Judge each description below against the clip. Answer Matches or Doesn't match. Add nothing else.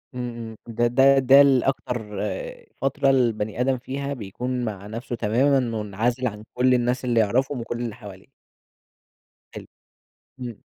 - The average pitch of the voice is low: Matches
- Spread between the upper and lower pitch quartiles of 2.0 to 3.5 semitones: Matches